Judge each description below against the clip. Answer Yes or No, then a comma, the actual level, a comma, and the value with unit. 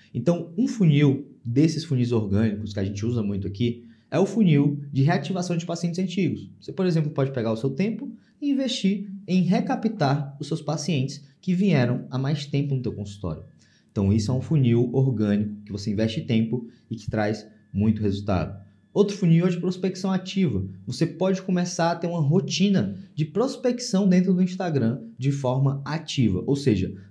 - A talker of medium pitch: Yes, medium, 145 Hz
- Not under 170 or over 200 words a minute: Yes, average, 180 wpm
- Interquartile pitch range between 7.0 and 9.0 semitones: Yes, wide, 8.4 semitones